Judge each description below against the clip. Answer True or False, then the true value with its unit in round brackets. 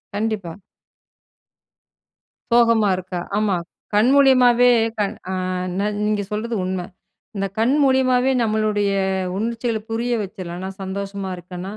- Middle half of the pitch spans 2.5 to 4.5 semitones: True (3.3 semitones)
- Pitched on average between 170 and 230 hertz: True (215 Hz)